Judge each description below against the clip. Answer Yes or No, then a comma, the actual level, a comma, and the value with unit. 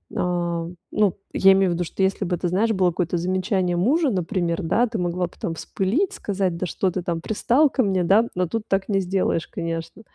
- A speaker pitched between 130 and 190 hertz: Yes, medium, 185 Hz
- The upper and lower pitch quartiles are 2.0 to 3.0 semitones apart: Yes, narrow, 2.6 semitones